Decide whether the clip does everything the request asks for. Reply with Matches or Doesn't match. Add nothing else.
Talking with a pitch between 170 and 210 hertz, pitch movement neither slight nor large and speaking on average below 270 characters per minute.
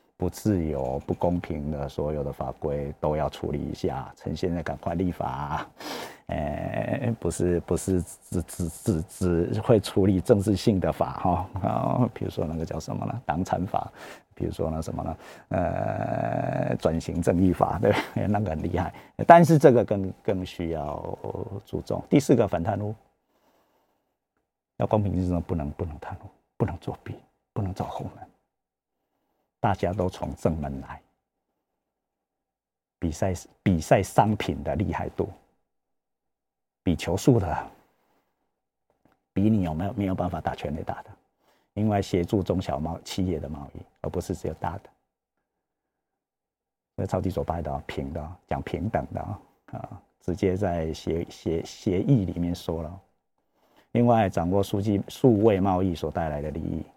Doesn't match